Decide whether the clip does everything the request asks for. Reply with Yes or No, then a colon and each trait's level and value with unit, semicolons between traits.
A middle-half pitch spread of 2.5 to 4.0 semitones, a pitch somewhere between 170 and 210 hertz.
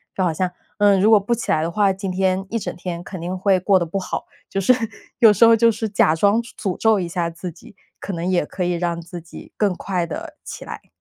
Yes: average, 2.9 semitones; high, 190 Hz